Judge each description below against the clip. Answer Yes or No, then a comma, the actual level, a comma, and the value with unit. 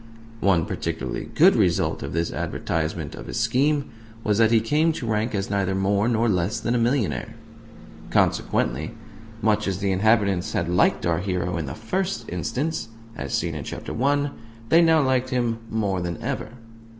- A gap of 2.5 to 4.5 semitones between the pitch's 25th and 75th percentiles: No, average, 5.3 semitones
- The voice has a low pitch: Yes, low, 105 Hz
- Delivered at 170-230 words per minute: Yes, average, 175 wpm